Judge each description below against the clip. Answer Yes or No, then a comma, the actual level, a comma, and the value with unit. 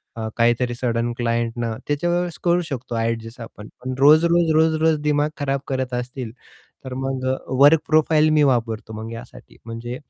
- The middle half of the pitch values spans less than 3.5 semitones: No, average, 4.9 semitones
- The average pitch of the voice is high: No, low, 130 Hz